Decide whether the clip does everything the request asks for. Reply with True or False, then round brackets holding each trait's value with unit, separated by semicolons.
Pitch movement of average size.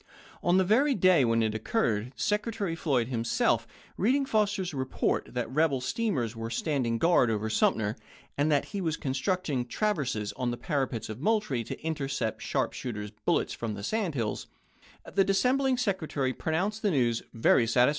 False (8.8 semitones)